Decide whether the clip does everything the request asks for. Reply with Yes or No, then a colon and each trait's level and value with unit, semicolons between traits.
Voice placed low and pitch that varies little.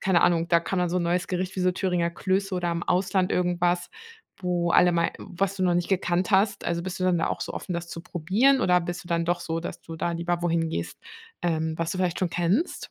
No: medium, 175 Hz; narrow, 1.5 semitones